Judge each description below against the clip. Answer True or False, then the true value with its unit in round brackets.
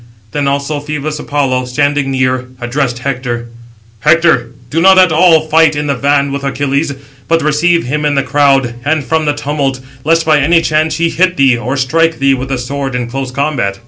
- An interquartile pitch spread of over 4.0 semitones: False (2.7 semitones)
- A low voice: False (145 Hz)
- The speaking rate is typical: True (195 wpm)